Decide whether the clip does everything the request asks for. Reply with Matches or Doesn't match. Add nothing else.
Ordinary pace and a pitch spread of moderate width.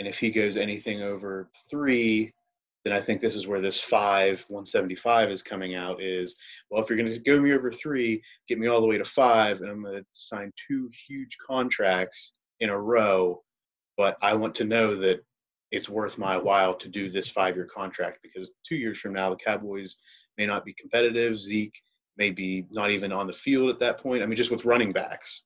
Doesn't match